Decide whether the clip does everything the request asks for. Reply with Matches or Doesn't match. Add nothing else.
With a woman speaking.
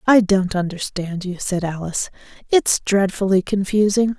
Matches